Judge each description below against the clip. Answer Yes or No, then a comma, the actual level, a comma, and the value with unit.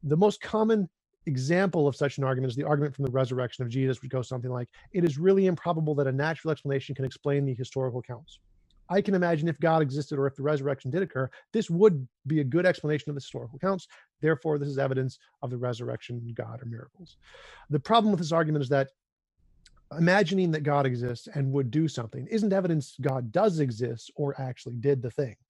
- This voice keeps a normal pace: No, fast, 210 wpm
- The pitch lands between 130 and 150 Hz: Yes, medium, 140 Hz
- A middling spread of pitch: Yes, average, 4.2 semitones